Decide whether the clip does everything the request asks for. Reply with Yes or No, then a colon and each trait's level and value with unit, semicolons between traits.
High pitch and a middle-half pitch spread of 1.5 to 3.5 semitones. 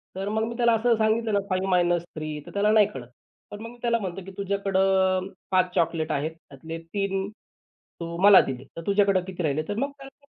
No: high, 195 Hz; average, 4.0 semitones